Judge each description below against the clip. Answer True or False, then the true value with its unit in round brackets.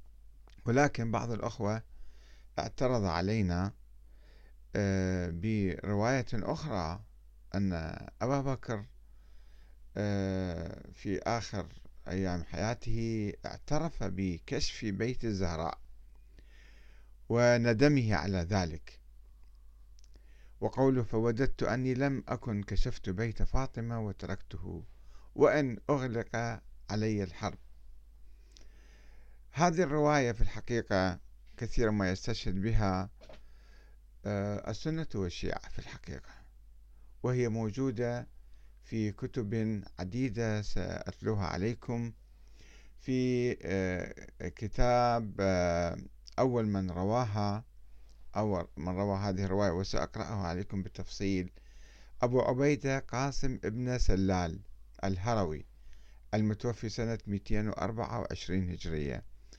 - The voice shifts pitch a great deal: True (6.2 semitones)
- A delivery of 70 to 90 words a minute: True (75 wpm)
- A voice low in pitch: True (100 Hz)